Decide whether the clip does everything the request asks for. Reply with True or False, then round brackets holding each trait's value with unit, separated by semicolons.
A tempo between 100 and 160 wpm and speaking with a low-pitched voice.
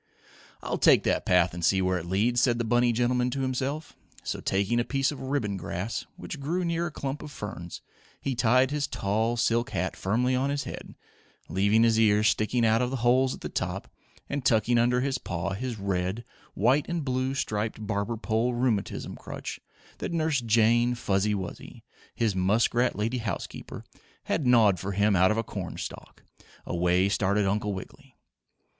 False (180 wpm; 115 Hz)